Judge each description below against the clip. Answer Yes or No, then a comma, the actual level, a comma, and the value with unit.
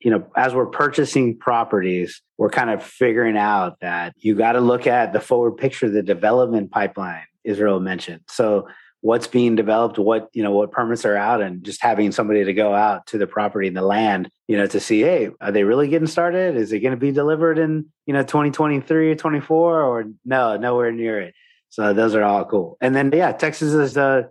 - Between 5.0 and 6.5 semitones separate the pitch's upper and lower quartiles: Yes, average, 5.3 semitones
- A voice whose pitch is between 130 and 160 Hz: No, low, 115 Hz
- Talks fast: Yes, fast, 215 wpm